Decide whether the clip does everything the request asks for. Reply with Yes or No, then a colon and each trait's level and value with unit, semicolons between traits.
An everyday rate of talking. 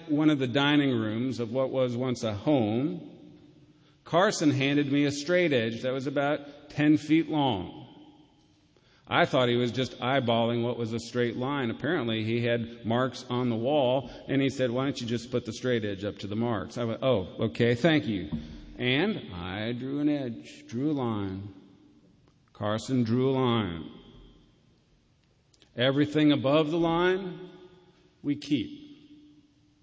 Yes: average, 160 wpm